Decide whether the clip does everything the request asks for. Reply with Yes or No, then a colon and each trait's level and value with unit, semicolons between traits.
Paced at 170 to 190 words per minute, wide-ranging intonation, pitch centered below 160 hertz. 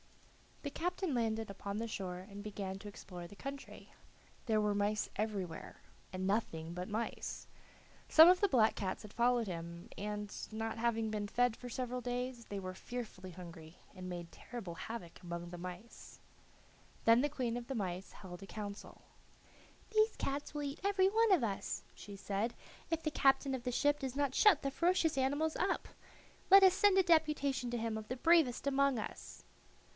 No: average, 180 wpm; wide, 6.0 semitones; high, 230 Hz